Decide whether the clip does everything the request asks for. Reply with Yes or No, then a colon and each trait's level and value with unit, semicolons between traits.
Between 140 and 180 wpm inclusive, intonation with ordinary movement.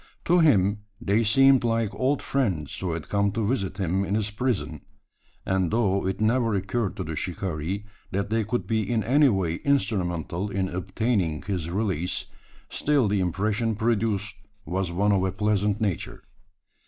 Yes: average, 165 wpm; average, 3.3 semitones